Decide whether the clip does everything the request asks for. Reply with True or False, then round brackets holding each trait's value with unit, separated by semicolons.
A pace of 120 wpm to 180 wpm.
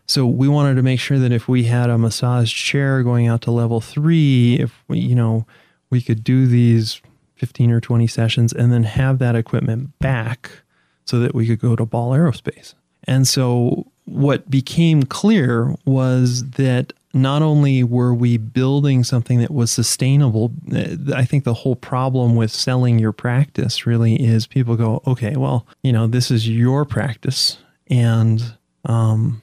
True (170 wpm)